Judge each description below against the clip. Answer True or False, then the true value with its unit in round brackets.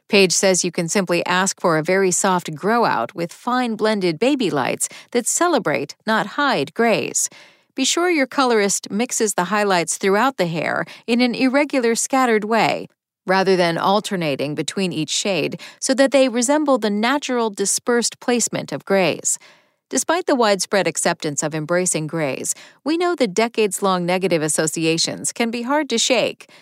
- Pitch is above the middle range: True (205 Hz)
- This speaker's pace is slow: False (160 wpm)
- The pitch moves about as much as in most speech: False (5.7 semitones)